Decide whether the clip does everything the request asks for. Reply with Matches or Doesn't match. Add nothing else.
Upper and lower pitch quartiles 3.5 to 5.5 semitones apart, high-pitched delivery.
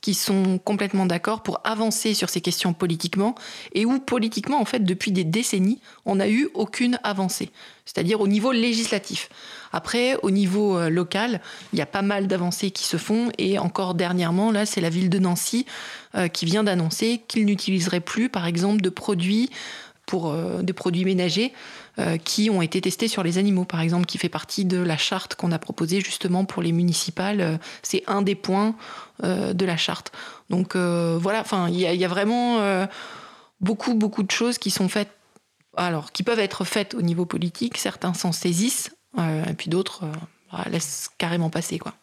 Doesn't match